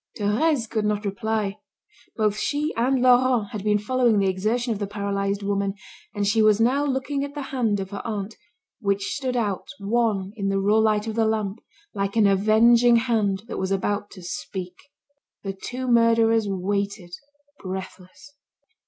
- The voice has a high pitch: Yes, high, 210 Hz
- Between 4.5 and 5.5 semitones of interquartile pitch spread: No, average, 2.9 semitones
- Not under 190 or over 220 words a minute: No, average, 170 wpm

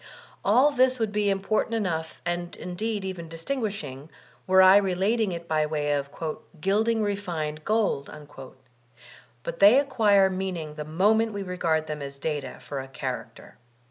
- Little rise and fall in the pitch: No, average, 5.3 semitones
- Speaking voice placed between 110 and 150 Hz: No, medium, 185 Hz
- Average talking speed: Yes, average, 150 wpm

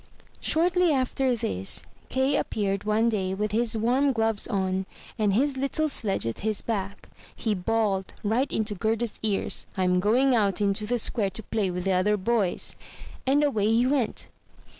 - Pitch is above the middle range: Yes, high, 215 Hz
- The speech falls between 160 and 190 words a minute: Yes, average, 165 wpm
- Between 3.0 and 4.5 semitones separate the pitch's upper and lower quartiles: Yes, average, 3.8 semitones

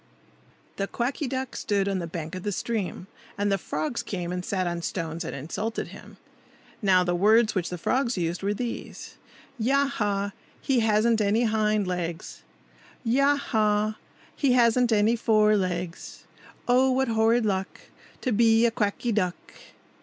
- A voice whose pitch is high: Yes, high, 210 Hz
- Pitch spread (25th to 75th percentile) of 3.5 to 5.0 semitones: Yes, average, 4.2 semitones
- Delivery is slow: No, average, 160 wpm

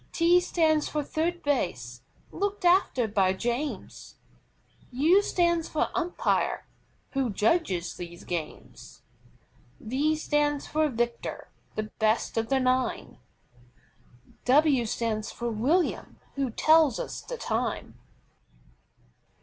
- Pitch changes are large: Yes, wide, 6.2 semitones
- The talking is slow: Yes, slow, 110 wpm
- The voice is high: Yes, very high, 270 Hz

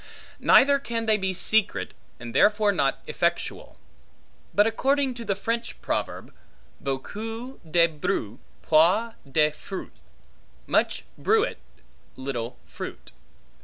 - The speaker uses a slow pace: Yes, slow, 110 wpm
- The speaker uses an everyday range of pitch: No, wide, 7.2 semitones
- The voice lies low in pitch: No, high, 205 Hz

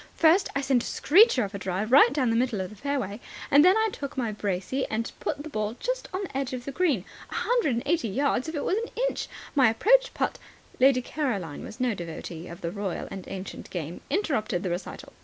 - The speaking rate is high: Yes, fast, 235 wpm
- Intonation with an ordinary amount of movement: No, wide, 6.7 semitones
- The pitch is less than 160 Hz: No, very high, 255 Hz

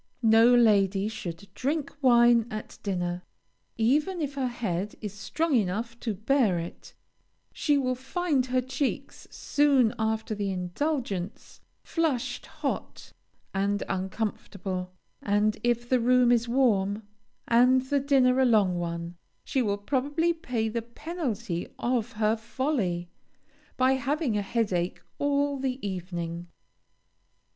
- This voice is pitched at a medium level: No, high, 235 Hz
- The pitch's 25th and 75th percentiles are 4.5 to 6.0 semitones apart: Yes, average, 4.8 semitones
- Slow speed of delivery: Yes, slow, 125 wpm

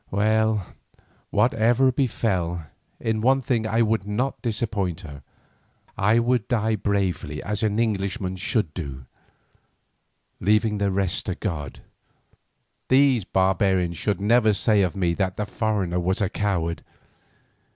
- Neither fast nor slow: No, slow, 130 wpm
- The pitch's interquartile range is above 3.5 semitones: No, average, 3.2 semitones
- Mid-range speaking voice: No, low, 105 Hz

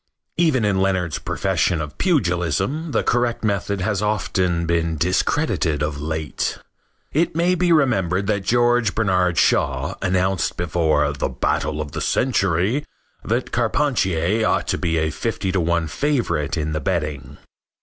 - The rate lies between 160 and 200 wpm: No, average, 145 wpm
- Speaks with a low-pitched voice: Yes, very low, 95 Hz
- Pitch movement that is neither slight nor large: No, wide, 6.0 semitones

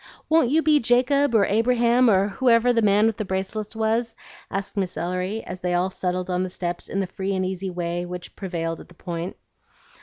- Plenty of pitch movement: No, average, 4.1 semitones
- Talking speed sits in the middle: No, fast, 210 wpm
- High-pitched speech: Yes, high, 195 Hz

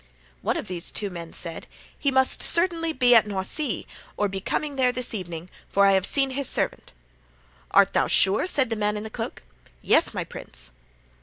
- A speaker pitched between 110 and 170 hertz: No, high, 215 Hz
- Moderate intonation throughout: No, wide, 5.7 semitones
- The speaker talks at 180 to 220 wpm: Yes, average, 190 wpm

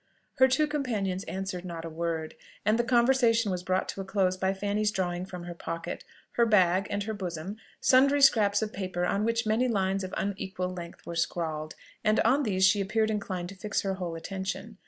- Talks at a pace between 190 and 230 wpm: Yes, average, 200 wpm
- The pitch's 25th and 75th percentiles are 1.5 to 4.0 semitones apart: Yes, average, 3.2 semitones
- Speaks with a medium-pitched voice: No, high, 195 Hz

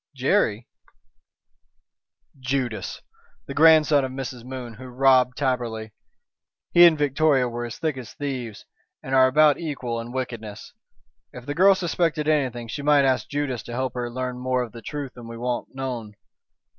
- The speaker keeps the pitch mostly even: No, average, 3.2 semitones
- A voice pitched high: No, low, 130 Hz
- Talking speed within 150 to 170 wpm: Yes, average, 165 wpm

